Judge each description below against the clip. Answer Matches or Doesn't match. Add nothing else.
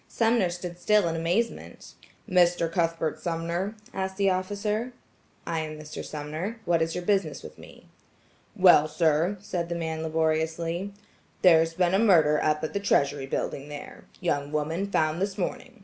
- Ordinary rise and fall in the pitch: Matches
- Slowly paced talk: Doesn't match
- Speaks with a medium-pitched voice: Matches